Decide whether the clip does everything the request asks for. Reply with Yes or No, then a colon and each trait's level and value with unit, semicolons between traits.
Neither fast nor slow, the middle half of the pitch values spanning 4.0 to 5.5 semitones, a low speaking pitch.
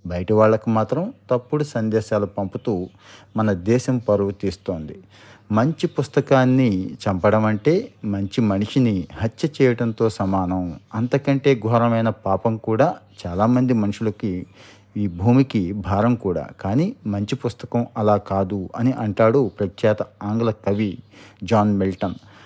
No: average, 110 wpm; average, 3.3 semitones; low, 110 Hz